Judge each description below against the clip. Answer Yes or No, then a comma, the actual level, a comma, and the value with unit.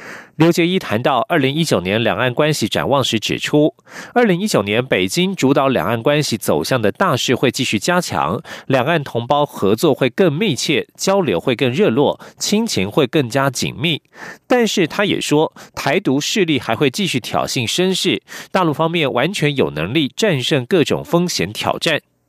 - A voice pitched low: No, medium, 155 Hz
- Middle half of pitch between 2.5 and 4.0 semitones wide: No, average, 5.0 semitones